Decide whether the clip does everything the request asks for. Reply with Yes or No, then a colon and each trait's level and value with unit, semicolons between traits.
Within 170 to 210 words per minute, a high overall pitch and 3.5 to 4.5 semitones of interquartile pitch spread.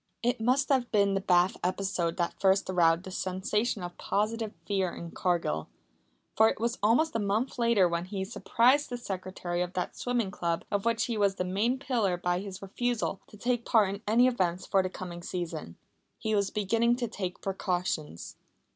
Yes: average, 190 wpm; high, 195 Hz; average, 4.2 semitones